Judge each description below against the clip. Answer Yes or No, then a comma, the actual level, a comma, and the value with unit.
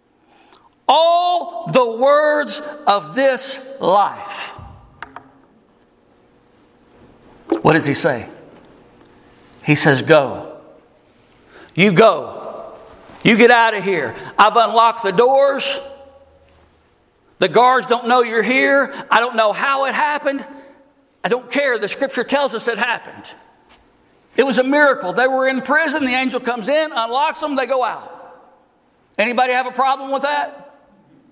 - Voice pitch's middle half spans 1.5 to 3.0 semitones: No, average, 5.1 semitones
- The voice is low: No, very high, 255 Hz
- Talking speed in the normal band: No, slow, 130 wpm